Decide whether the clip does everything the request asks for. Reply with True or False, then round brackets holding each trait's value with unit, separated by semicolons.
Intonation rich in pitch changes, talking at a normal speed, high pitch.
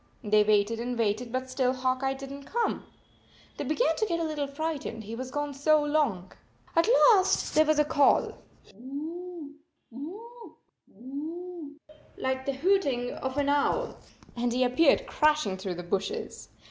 False (4.0 semitones; 165 wpm; 280 Hz)